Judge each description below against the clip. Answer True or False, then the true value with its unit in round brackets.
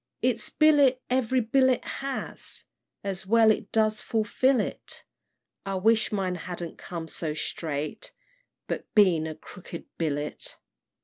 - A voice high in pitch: True (210 Hz)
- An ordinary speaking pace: False (125 wpm)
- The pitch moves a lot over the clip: True (6.5 semitones)